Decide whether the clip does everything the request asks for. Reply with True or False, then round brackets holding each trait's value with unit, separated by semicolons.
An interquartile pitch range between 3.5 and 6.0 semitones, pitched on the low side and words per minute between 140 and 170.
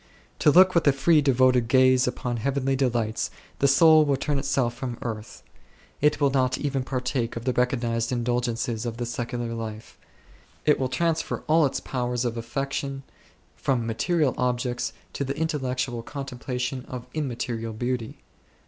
False (2.4 semitones; 125 Hz; 155 wpm)